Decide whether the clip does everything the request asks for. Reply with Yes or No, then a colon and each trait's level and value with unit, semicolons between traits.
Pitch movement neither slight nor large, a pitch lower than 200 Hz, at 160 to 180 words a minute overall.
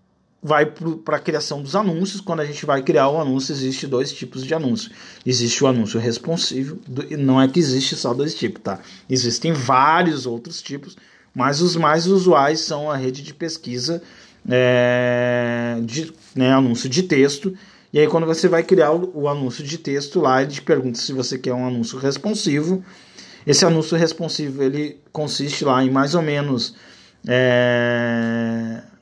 Yes: average, 4.3 semitones; medium, 140 Hz; average, 170 wpm